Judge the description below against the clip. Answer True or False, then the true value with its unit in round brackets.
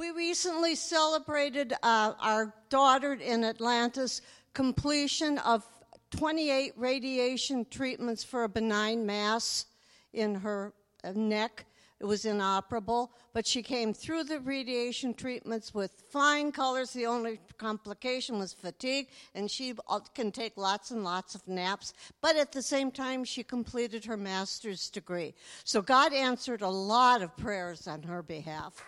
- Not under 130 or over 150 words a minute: True (140 wpm)